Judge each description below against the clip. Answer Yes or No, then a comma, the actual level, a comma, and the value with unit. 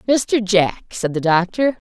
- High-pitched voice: Yes, high, 205 Hz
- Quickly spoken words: No, average, 160 wpm